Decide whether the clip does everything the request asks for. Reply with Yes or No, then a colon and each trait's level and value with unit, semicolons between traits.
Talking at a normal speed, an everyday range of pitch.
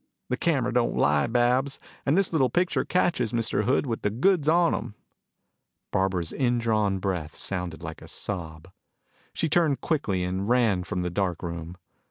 No: average, 165 wpm; wide, 6.9 semitones